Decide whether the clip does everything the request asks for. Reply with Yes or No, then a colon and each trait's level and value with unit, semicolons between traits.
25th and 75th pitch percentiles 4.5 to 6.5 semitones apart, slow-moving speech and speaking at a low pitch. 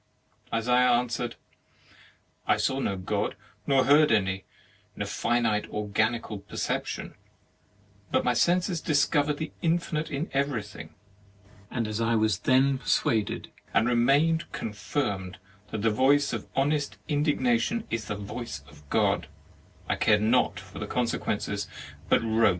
Yes: average, 5.0 semitones; slow, 130 wpm; low, 120 Hz